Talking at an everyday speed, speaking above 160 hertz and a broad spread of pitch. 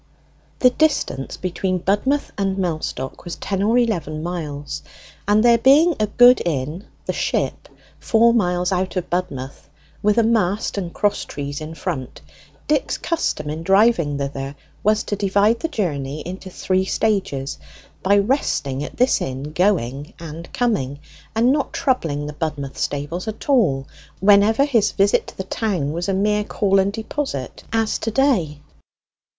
Yes: average, 155 wpm; high, 190 Hz; wide, 6.6 semitones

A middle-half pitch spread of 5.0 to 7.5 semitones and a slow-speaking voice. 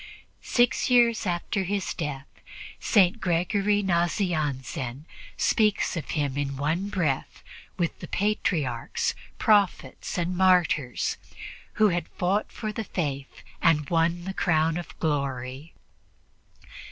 Yes: average, 5.3 semitones; slow, 115 wpm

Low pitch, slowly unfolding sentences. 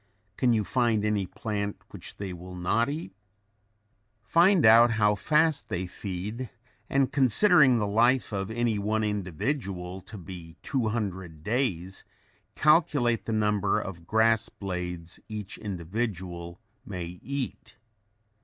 Yes: low, 105 Hz; slow, 125 wpm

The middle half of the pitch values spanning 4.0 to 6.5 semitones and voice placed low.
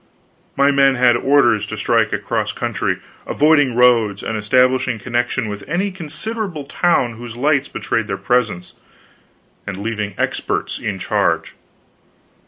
Yes: average, 4.6 semitones; low, 125 Hz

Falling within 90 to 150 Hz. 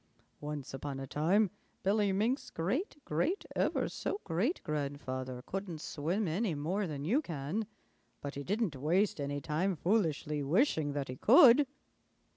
No: medium, 165 Hz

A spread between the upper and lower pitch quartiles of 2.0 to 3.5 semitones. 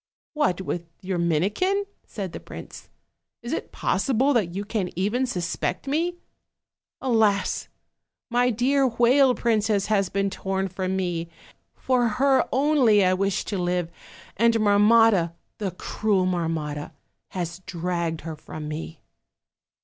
No: average, 5.1 semitones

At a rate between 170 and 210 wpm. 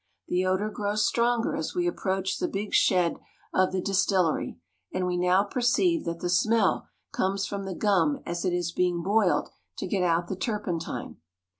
Yes: average, 175 wpm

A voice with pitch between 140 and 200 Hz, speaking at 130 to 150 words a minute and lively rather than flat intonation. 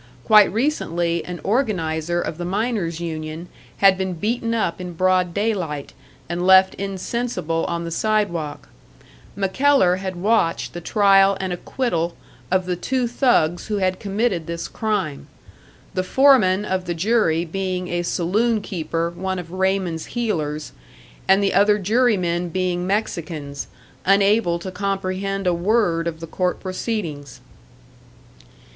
No: medium, 185 Hz; average, 140 wpm; average, 3.3 semitones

